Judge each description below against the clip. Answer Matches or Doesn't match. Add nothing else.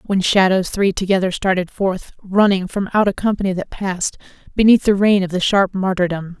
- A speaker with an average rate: Matches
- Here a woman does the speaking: Matches